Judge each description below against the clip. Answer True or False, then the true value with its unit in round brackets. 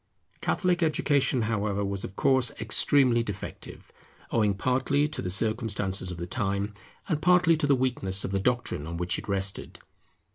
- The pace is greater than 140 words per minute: True (160 wpm)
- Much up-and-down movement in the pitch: True (5.7 semitones)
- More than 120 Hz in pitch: False (110 Hz)